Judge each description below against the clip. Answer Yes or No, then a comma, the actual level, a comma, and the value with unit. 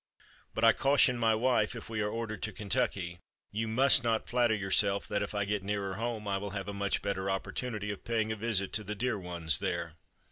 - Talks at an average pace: No, fast, 220 wpm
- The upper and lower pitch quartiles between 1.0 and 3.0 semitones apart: Yes, narrow, 2.5 semitones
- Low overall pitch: Yes, low, 105 Hz